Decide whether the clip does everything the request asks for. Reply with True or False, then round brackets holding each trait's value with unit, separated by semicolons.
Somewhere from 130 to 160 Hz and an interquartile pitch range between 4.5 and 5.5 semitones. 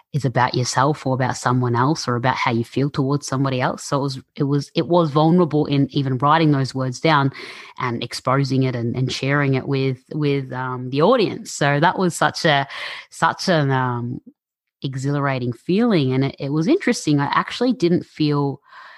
False (140 Hz; 2.9 semitones)